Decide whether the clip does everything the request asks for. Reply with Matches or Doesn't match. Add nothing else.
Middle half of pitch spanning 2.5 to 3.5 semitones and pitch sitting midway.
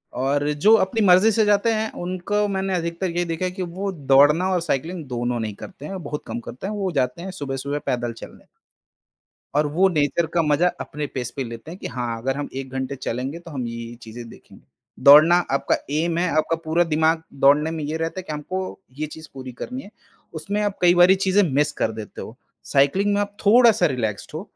Doesn't match